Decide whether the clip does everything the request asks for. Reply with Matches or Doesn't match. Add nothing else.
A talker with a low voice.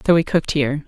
Doesn't match